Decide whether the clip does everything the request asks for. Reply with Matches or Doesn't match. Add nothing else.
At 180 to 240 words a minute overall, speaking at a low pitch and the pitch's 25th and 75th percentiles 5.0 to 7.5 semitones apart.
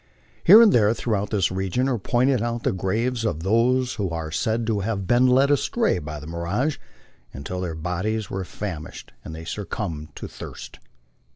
Matches